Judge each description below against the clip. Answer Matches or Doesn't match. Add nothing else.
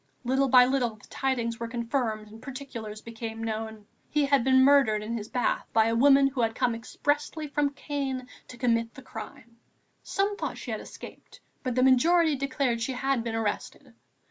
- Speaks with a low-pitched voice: Doesn't match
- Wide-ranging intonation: Doesn't match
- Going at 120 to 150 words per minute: Doesn't match